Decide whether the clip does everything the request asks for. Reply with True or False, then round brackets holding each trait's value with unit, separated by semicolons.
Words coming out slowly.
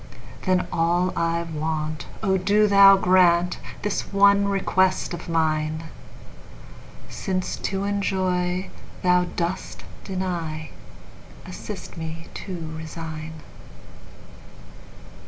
True (75 wpm)